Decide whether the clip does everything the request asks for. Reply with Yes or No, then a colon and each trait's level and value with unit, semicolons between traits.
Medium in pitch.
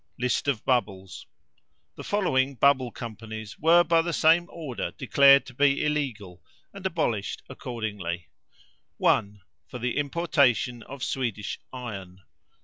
No: low, 125 Hz